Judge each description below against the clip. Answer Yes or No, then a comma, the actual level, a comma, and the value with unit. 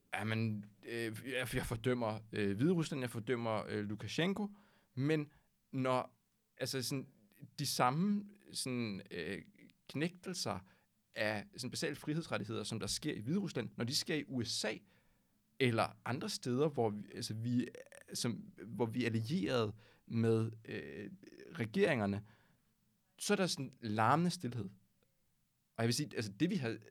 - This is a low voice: Yes, low, 125 Hz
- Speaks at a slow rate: Yes, slow, 135 wpm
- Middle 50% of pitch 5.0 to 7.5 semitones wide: Yes, wide, 5.4 semitones